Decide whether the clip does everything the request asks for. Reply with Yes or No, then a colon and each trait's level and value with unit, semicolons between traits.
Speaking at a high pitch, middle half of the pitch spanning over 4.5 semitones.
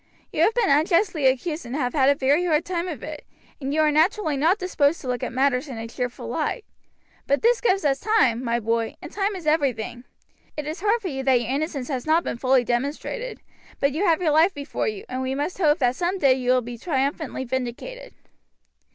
Yes: very high, 290 Hz; average, 5.2 semitones